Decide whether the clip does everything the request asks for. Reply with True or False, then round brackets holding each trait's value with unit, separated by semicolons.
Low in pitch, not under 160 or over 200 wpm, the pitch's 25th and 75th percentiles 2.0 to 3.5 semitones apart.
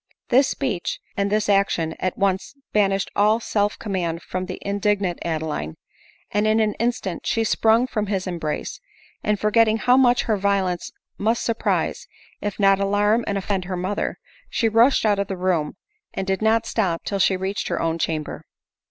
False (200 Hz; 180 wpm; 2.8 semitones)